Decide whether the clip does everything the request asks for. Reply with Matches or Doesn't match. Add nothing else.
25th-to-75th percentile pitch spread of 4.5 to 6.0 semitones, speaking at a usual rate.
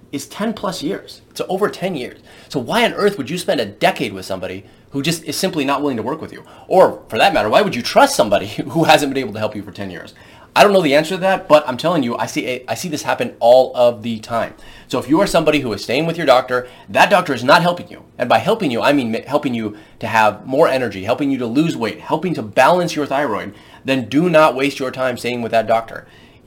Doesn't match